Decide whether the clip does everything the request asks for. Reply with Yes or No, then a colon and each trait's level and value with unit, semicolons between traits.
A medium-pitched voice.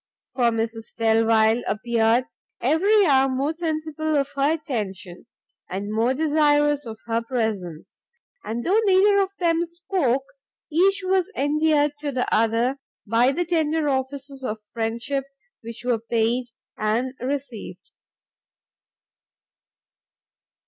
No: very high, 265 Hz